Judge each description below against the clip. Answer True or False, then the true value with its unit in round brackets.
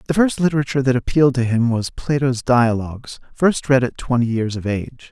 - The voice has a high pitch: False (125 Hz)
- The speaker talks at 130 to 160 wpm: False (200 wpm)